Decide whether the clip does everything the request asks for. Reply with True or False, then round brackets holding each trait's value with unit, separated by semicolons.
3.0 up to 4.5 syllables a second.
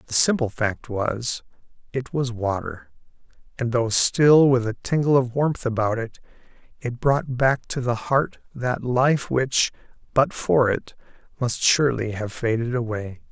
True (4.1 syllables/s)